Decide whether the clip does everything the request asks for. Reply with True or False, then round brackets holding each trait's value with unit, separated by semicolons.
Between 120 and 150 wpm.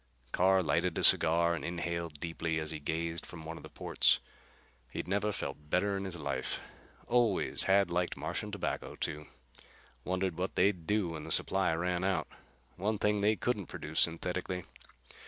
False (170 wpm)